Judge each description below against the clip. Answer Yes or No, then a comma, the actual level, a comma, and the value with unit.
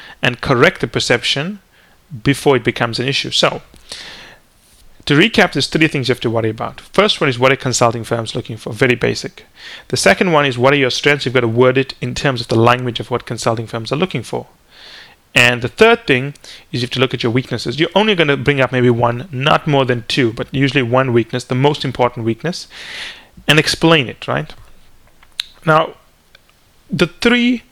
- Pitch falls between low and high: No, low, 130 Hz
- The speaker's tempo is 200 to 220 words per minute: Yes, fast, 205 wpm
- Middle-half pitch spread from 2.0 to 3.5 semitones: Yes, average, 3.1 semitones